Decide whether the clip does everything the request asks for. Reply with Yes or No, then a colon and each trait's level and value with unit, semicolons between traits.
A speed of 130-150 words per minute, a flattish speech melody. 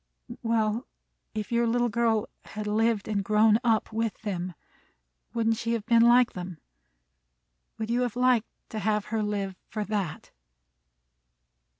Yes: average, 140 wpm; narrow, 1.8 semitones